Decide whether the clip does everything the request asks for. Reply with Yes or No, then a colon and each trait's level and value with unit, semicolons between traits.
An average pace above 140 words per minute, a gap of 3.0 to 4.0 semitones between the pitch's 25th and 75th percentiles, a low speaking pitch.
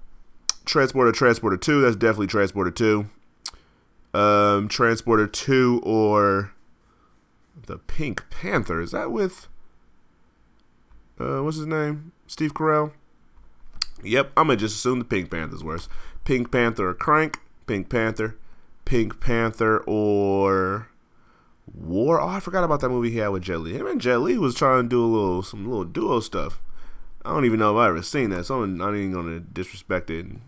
No: average, 160 wpm; average, 4.4 semitones; low, 110 Hz